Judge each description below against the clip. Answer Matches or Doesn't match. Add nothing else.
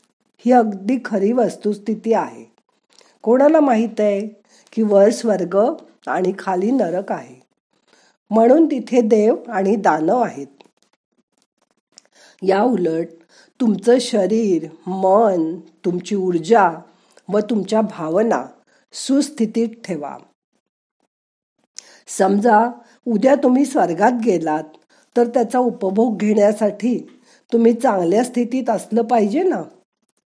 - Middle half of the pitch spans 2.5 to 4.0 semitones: Matches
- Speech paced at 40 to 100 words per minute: Matches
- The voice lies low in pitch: Doesn't match